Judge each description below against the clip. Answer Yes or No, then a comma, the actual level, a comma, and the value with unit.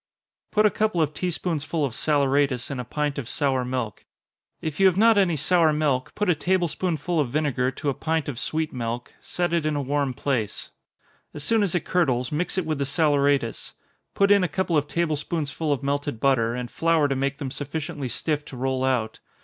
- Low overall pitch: No, medium, 145 Hz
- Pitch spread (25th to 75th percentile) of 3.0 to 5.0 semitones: Yes, average, 3.9 semitones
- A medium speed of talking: No, fast, 215 wpm